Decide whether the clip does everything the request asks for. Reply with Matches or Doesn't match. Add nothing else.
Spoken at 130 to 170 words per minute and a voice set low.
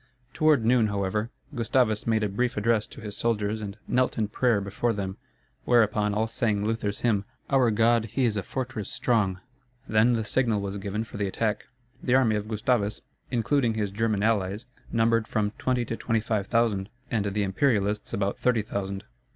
Doesn't match